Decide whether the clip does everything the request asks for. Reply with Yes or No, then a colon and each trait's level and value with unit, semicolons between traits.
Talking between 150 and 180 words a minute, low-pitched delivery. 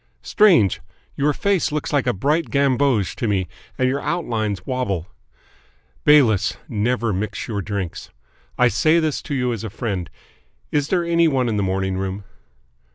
Yes: average, 160 wpm; low, 125 Hz